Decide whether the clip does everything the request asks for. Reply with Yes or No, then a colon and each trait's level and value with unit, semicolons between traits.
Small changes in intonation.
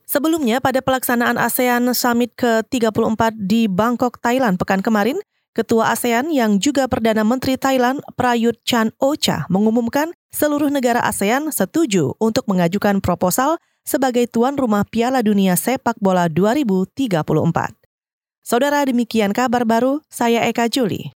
No: average, 3.3 semitones